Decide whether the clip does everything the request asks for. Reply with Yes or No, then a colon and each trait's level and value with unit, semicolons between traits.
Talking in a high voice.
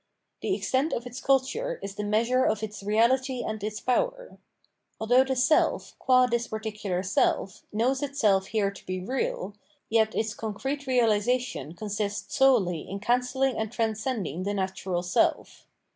Yes: high, 220 Hz